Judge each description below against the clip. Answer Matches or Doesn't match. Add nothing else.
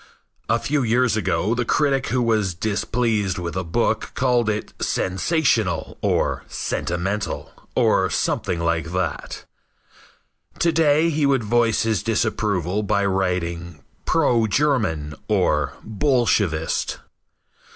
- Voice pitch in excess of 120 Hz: Doesn't match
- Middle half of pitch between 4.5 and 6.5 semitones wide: Matches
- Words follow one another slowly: Matches